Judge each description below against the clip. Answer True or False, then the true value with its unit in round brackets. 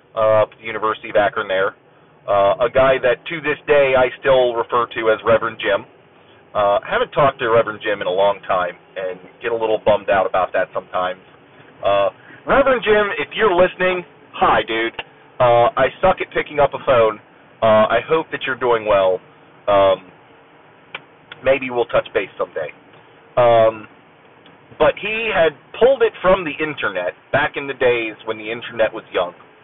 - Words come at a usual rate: True (175 wpm)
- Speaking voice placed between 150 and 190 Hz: False (120 Hz)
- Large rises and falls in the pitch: True (5.7 semitones)